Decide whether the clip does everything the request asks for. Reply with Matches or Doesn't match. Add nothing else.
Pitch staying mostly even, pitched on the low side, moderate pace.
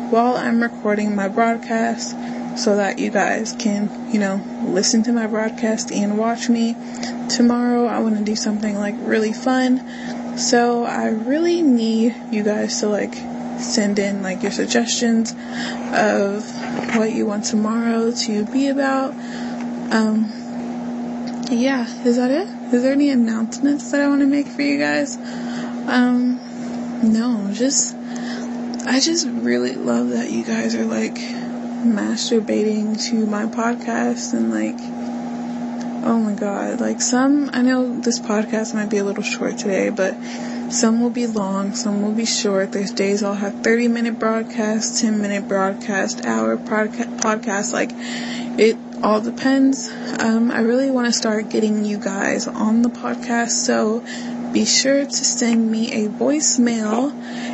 Doesn't match